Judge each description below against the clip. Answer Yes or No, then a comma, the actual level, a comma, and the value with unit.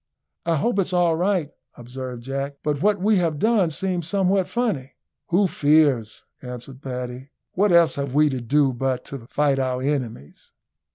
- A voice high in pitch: No, medium, 145 Hz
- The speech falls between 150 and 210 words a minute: Yes, average, 165 wpm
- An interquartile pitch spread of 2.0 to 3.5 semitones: No, wide, 5.5 semitones